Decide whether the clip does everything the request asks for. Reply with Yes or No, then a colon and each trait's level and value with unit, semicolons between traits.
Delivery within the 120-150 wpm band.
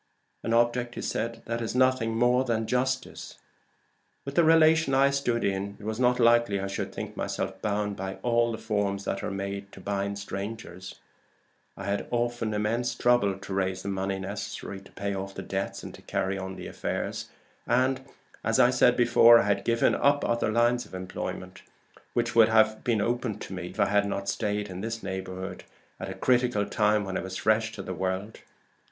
No: average, 190 wpm